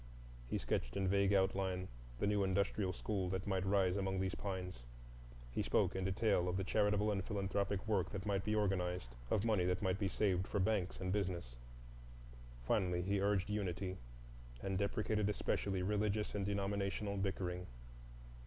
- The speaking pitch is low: Yes, very low, 95 Hz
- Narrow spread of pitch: Yes, narrow, 1.7 semitones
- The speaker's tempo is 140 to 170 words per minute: Yes, average, 160 wpm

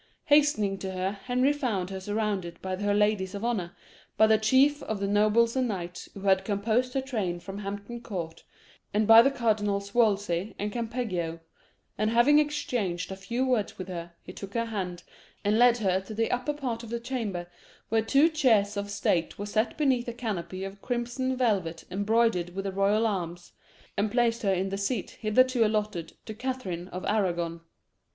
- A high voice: Yes, high, 210 Hz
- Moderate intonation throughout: Yes, average, 3.8 semitones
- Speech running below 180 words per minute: No, average, 185 wpm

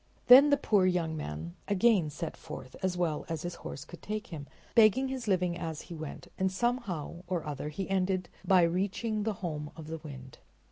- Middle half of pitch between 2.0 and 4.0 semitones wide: No, average, 4.5 semitones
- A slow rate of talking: No, average, 195 wpm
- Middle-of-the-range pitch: Yes, medium, 180 Hz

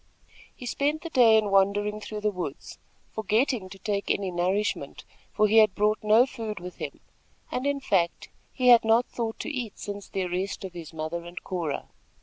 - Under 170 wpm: No, average, 190 wpm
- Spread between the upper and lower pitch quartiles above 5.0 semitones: No, average, 3.4 semitones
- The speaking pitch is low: No, high, 210 Hz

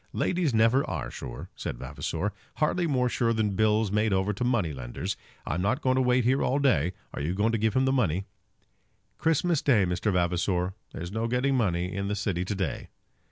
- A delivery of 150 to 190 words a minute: No, fast, 205 wpm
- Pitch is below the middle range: Yes, low, 105 Hz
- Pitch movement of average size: No, wide, 5.8 semitones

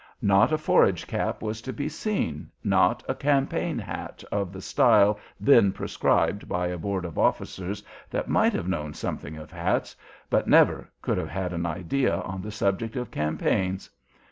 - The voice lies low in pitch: Yes, very low, 95 Hz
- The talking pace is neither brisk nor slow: Yes, average, 170 wpm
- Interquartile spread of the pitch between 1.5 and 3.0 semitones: No, average, 3.8 semitones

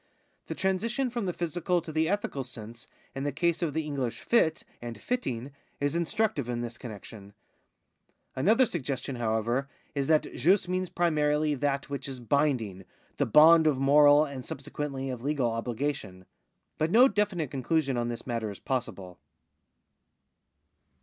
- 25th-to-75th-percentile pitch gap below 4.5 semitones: No, wide, 5.4 semitones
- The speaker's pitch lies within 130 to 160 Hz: Yes, medium, 140 Hz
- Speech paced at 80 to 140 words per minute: No, average, 155 wpm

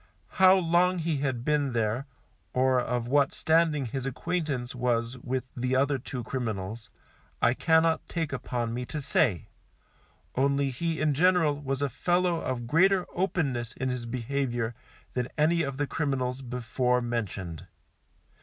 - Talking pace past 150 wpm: No, average, 145 wpm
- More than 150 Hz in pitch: No, low, 135 Hz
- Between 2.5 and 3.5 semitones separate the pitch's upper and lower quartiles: No, average, 4.3 semitones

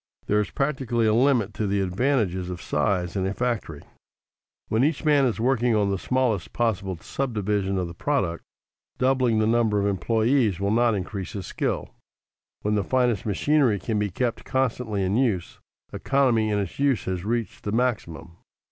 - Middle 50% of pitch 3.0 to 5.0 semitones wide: Yes, average, 4.3 semitones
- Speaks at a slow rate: No, average, 175 wpm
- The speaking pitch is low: Yes, low, 110 Hz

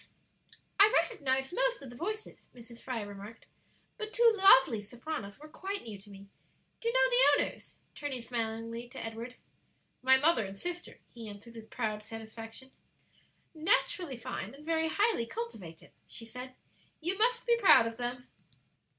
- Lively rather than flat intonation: Yes, wide, 7.6 semitones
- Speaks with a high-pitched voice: Yes, very high, 250 Hz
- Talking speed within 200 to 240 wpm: No, average, 160 wpm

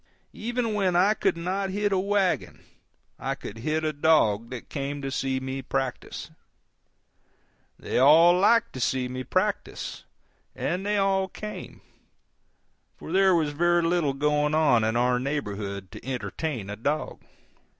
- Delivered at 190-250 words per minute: No, average, 150 wpm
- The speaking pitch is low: No, medium, 150 Hz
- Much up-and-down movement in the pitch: Yes, wide, 6.5 semitones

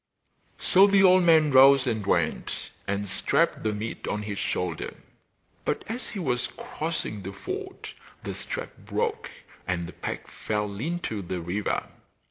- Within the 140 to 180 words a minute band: Yes, average, 150 wpm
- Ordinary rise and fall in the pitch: No, wide, 8.3 semitones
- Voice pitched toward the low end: Yes, low, 110 Hz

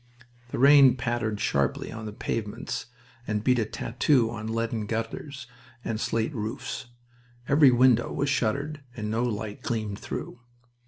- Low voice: Yes, low, 115 Hz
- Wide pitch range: No, average, 3.0 semitones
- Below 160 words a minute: Yes, average, 145 wpm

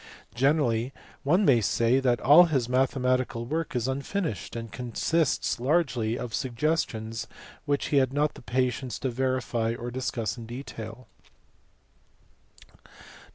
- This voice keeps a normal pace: No, slow, 130 wpm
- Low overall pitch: Yes, low, 125 Hz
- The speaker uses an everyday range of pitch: Yes, average, 3.1 semitones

